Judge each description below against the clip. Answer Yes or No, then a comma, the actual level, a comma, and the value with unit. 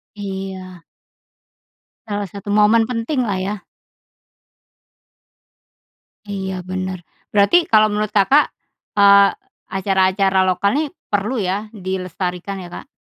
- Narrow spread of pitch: Yes, narrow, 1.9 semitones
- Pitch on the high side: Yes, high, 200 Hz